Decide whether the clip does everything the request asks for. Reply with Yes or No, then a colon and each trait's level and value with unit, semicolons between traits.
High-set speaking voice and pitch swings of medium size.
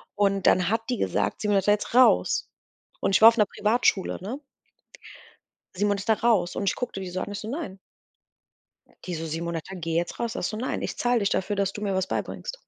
Yes: high, 205 Hz; average, 3.3 semitones